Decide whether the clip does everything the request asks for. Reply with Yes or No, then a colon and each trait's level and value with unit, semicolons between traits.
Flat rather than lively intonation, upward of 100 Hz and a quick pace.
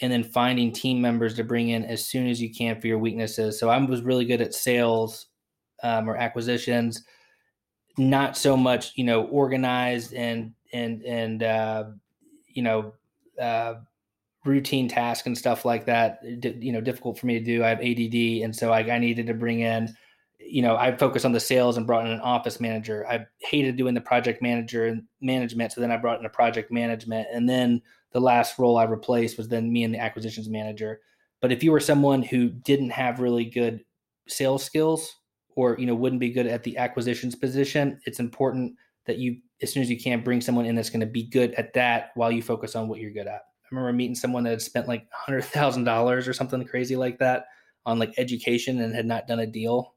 Yes: narrow, 1.6 semitones; low, 120 Hz; fast, 215 wpm